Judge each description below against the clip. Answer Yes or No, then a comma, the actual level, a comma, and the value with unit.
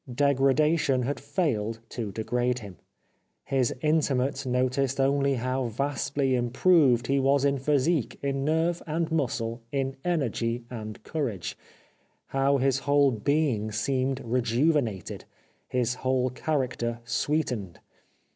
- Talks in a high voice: No, low, 135 Hz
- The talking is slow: Yes, slow, 115 wpm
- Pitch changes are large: No, average, 2.8 semitones